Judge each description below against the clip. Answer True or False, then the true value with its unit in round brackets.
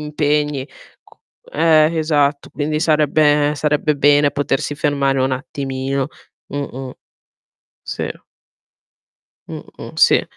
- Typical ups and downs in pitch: False (1.6 semitones)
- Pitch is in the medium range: True (145 Hz)